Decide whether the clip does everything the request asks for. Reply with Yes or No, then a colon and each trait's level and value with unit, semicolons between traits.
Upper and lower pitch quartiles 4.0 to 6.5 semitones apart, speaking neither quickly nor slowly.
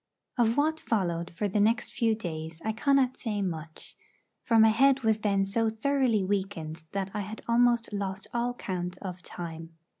Yes: average, 4.4 semitones; average, 175 wpm